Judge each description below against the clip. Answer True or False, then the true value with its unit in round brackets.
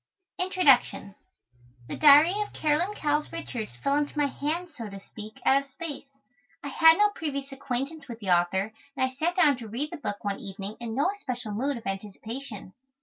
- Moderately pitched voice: False (275 Hz)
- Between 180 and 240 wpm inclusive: True (190 wpm)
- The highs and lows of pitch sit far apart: True (5.7 semitones)